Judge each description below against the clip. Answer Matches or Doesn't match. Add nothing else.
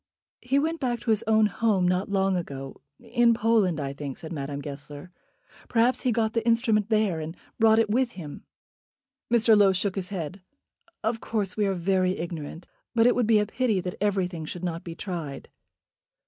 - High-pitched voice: Matches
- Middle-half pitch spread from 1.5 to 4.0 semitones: Doesn't match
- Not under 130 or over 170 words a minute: Doesn't match